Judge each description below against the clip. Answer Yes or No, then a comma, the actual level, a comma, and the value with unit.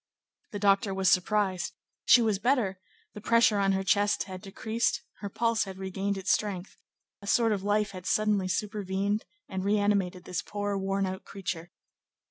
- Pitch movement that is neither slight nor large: No, narrow, 1.6 semitones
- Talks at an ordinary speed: Yes, average, 165 wpm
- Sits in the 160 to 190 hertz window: No, high, 200 Hz